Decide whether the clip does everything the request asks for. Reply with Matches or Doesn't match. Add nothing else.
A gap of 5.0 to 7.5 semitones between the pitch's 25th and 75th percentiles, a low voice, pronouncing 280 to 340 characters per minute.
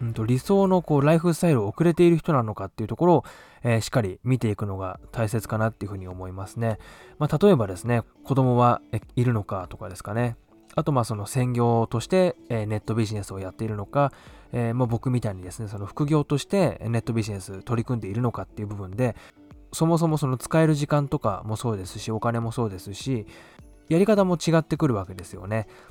Doesn't match